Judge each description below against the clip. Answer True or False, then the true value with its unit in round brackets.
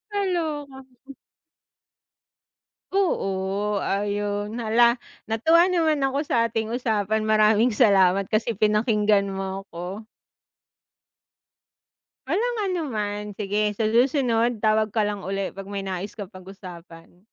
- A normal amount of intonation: True (3.4 semitones)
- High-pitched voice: True (215 Hz)